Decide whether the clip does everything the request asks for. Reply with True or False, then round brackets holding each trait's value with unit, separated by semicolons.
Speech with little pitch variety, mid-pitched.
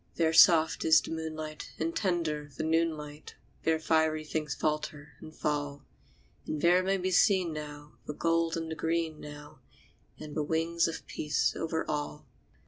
True (1.6 semitones; 160 Hz)